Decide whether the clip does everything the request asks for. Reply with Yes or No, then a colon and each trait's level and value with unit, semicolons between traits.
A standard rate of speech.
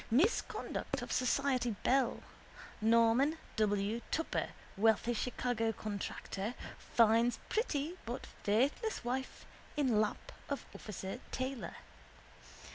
No: slow, 95 wpm